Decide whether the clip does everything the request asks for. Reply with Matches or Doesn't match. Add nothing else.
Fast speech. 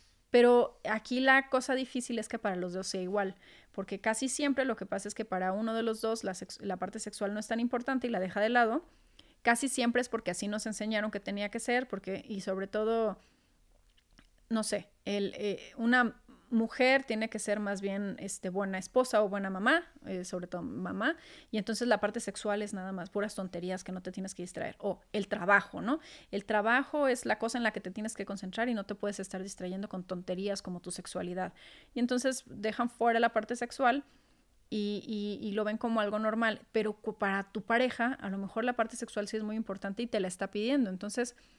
Matches